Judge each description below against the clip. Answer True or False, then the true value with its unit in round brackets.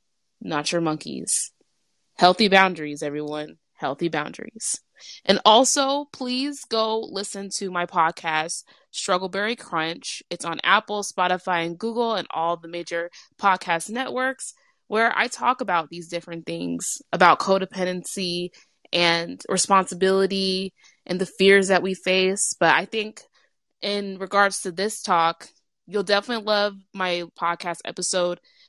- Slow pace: True (130 wpm)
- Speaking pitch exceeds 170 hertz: True (190 Hz)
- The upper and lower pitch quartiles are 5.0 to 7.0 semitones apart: False (3.3 semitones)